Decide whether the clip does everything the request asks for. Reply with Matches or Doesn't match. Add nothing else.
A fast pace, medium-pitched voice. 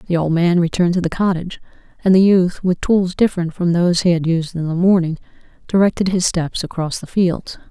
Matches